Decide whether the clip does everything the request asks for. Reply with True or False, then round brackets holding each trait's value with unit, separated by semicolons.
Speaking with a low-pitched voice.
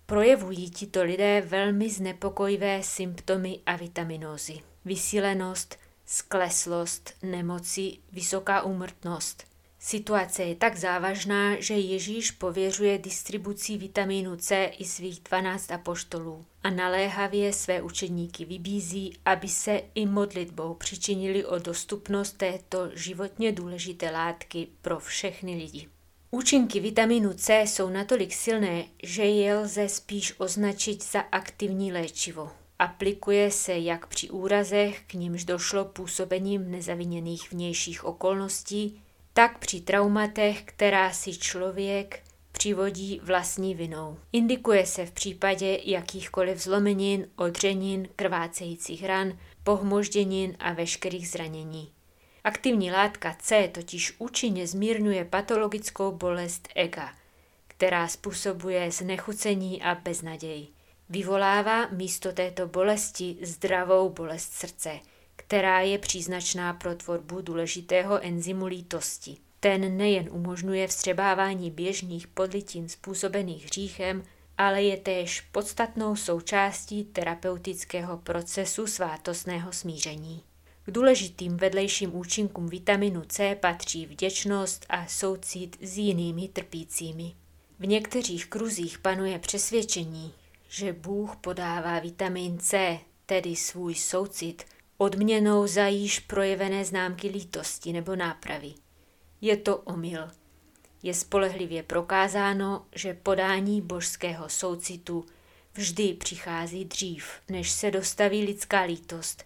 False (190 Hz)